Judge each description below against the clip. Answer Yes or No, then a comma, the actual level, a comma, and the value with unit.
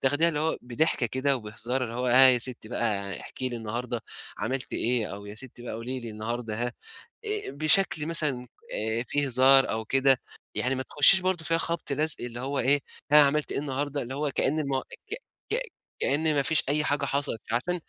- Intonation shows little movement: No, average, 3.7 semitones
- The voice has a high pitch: No, low, 130 Hz